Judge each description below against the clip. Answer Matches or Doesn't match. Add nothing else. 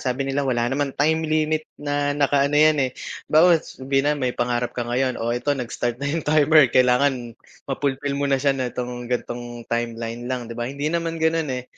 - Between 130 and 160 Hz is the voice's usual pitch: Matches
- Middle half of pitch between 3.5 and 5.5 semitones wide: Doesn't match